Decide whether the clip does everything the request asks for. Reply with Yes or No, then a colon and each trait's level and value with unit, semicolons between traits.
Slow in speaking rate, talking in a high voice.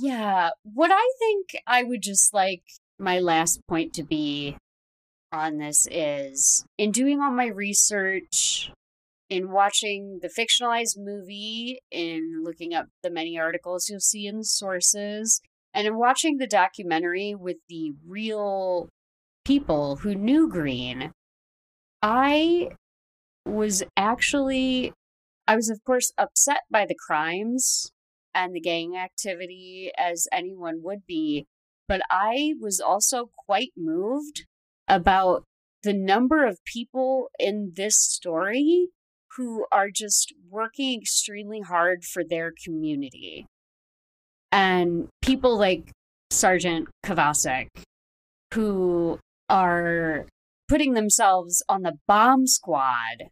Yes: slow, 115 wpm; high, 195 Hz